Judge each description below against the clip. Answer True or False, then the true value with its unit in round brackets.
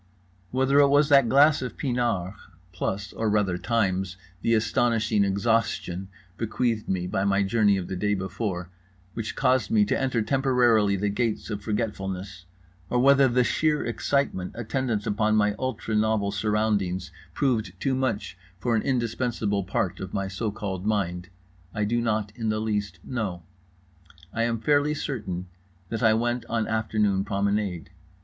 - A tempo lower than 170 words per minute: True (155 wpm)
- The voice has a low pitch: True (110 Hz)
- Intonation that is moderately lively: True (3.6 semitones)